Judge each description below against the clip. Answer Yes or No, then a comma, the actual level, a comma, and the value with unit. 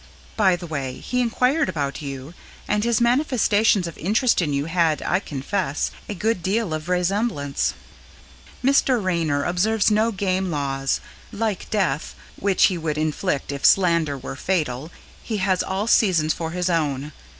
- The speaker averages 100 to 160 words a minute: Yes, average, 155 wpm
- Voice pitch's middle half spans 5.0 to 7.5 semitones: Yes, wide, 5.5 semitones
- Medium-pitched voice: Yes, medium, 180 Hz